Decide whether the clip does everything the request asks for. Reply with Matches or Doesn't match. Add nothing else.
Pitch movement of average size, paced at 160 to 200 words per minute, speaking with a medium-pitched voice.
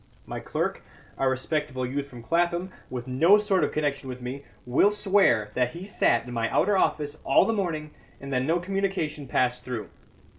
Doesn't match